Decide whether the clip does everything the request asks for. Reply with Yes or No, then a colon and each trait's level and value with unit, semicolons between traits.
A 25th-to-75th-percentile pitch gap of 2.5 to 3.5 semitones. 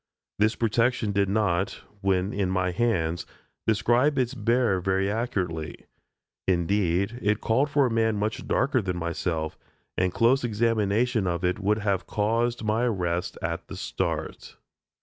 No: average, 4.1 semitones